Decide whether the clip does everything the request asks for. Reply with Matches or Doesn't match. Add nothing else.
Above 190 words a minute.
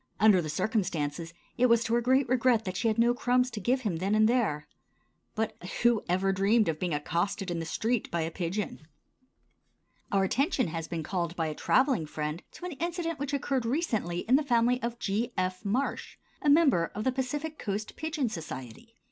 Matches